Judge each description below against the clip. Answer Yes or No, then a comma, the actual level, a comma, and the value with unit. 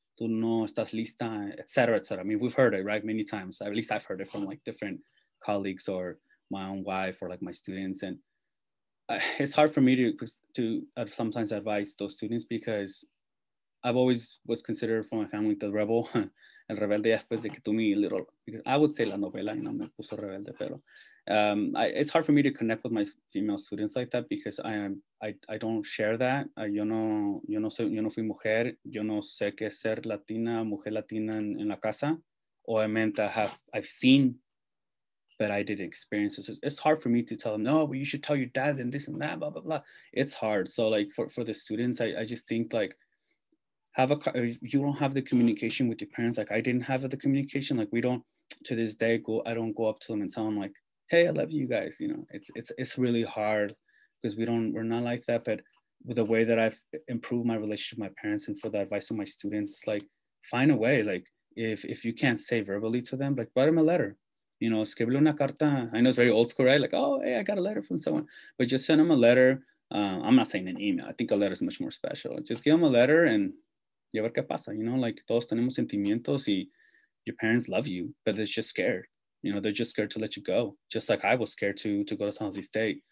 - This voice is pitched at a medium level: No, low, 115 Hz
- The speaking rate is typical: No, fast, 240 wpm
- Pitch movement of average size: Yes, average, 3.5 semitones